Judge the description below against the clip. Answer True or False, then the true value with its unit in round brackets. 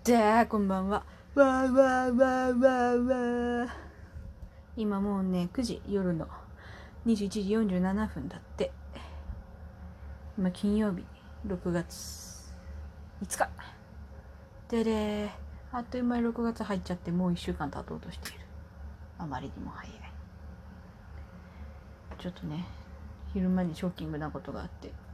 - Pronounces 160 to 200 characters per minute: True (195 characters per minute)